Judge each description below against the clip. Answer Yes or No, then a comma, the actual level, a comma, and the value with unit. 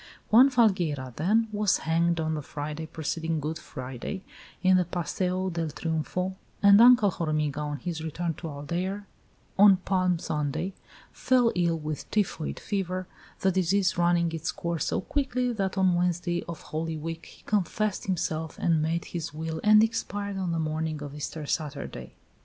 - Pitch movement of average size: Yes, average, 3.3 semitones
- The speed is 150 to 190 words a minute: Yes, average, 160 wpm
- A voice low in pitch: No, medium, 170 Hz